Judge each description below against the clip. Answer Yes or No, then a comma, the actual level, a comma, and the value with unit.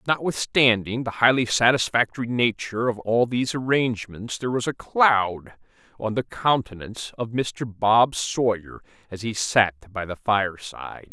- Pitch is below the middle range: Yes, low, 115 Hz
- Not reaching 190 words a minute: Yes, average, 140 wpm